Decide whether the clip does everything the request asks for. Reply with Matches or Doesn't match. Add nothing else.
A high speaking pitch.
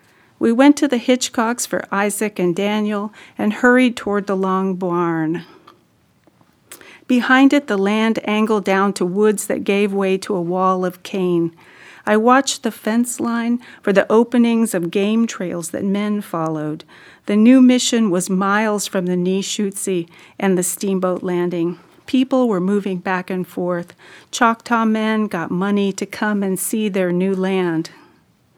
Matches